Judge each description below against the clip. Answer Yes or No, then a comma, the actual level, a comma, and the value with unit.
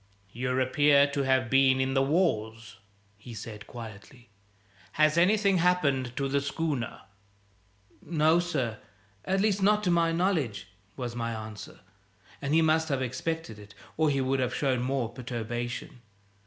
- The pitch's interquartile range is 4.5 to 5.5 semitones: Yes, average, 5.1 semitones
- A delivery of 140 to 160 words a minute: Yes, average, 150 wpm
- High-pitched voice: No, low, 135 Hz